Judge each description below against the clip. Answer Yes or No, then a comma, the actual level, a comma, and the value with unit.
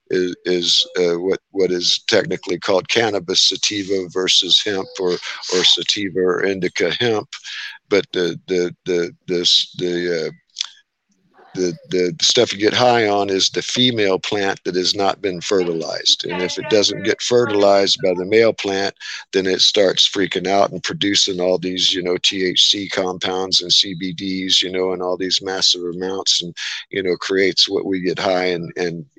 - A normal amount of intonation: No, narrow, 1.6 semitones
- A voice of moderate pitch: No, very low, 95 Hz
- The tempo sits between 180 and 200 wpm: No, average, 170 wpm